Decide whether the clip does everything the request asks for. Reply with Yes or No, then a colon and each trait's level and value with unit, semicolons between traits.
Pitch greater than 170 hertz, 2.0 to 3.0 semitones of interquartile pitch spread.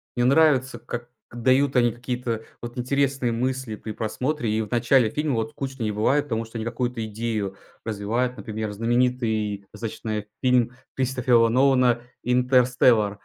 No: low, 120 Hz; narrow, 2.4 semitones